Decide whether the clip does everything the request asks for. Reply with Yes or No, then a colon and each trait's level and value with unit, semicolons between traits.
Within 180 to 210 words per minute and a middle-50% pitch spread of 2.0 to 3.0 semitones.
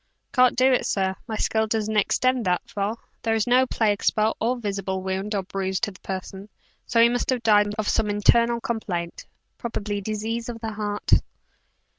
Yes: average, 185 wpm; average, 2.7 semitones